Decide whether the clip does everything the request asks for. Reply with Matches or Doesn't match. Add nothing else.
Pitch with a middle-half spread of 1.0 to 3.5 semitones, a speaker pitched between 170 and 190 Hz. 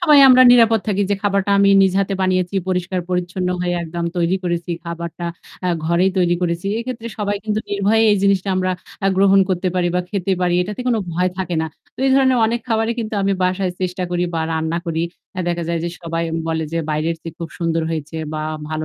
Matches